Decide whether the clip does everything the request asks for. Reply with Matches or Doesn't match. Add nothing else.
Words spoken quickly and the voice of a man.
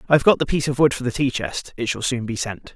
Matches